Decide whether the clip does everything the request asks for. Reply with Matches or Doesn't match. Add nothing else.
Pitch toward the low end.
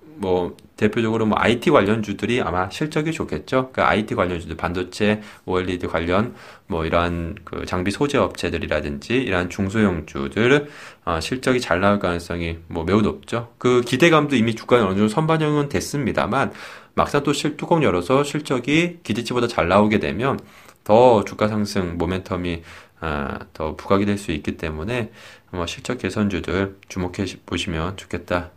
Matches